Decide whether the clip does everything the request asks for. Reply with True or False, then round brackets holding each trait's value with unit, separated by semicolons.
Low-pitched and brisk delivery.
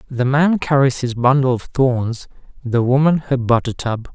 False (130 Hz; 175 wpm)